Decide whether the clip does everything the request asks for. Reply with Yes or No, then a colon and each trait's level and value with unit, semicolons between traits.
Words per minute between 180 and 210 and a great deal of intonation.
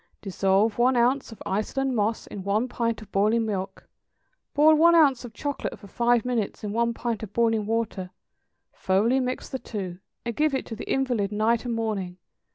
No: average, 190 wpm; average, 3.3 semitones